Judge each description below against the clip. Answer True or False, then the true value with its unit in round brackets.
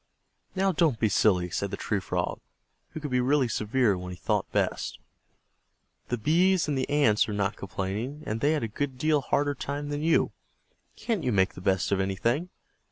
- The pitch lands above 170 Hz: False (125 Hz)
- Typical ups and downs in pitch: False (6.7 semitones)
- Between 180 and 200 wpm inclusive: True (195 wpm)